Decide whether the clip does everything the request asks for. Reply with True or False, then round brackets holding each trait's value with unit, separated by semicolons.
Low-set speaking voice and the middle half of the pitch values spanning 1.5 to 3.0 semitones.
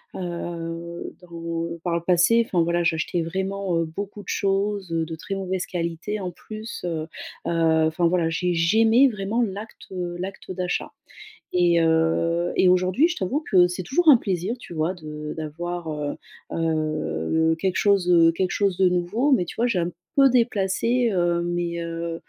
False (175 Hz; 2.7 semitones)